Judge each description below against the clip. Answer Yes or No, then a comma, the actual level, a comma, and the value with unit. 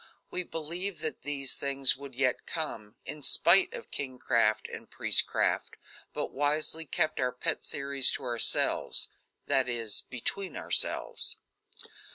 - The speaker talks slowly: Yes, slow, 130 wpm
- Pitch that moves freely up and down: No, average, 3.7 semitones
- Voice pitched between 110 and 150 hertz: Yes, medium, 140 Hz